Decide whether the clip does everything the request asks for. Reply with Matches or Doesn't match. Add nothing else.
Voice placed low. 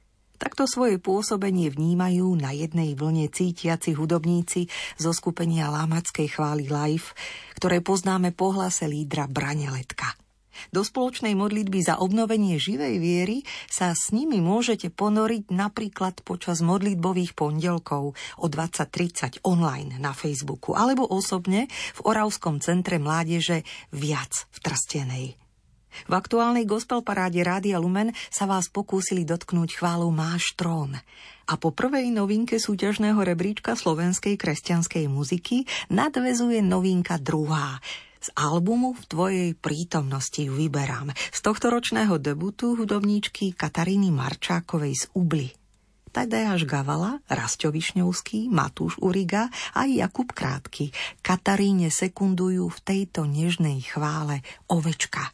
Doesn't match